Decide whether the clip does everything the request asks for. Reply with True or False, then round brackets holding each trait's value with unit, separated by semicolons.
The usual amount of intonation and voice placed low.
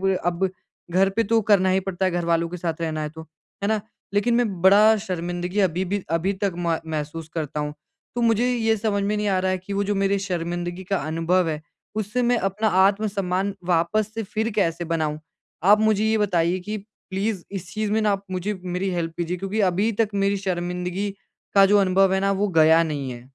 False (3.0 semitones; 190 Hz)